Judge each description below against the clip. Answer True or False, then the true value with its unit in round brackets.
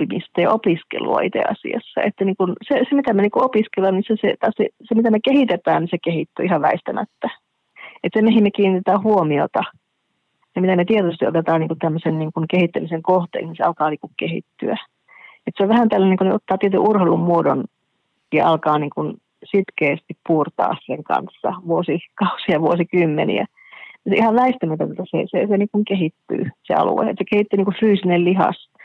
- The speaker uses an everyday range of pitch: True (3.7 semitones)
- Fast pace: True (180 wpm)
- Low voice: False (190 Hz)